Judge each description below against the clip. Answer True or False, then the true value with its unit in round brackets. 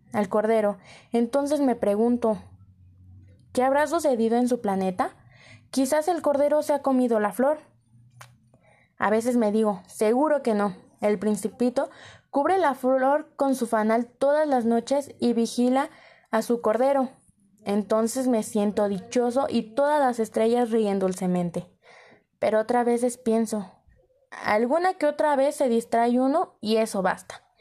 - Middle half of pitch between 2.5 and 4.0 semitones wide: False (4.5 semitones)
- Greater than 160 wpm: False (145 wpm)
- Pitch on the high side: True (235 Hz)